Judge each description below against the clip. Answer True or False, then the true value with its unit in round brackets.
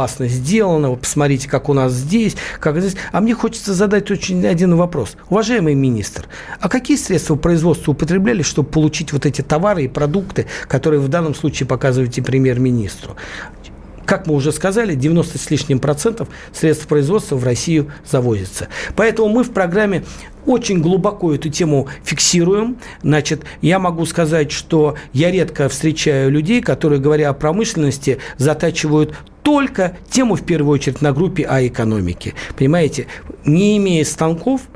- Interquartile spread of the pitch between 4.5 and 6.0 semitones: True (4.8 semitones)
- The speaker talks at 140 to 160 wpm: True (145 wpm)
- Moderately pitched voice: True (155 Hz)